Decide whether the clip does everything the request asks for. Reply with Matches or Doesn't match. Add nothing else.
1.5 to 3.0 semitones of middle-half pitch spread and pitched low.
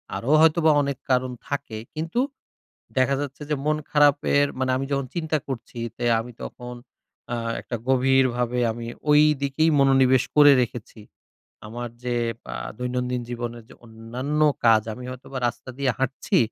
Matches